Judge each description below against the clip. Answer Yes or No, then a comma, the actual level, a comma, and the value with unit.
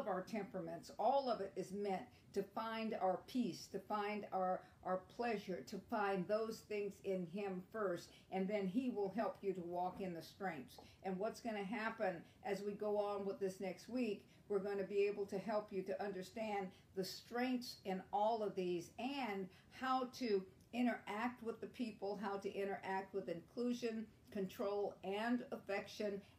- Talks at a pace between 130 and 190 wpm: Yes, average, 175 wpm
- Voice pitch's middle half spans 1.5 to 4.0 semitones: Yes, narrow, 2.6 semitones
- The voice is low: No, high, 200 Hz